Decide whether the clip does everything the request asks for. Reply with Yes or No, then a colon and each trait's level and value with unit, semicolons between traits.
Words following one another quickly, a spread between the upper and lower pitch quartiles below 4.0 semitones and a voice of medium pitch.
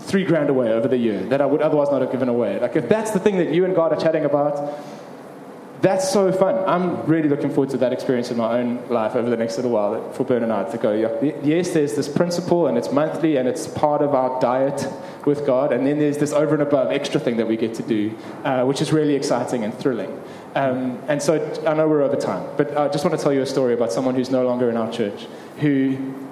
Yes: fast, 260 wpm; average, 3.4 semitones; medium, 145 Hz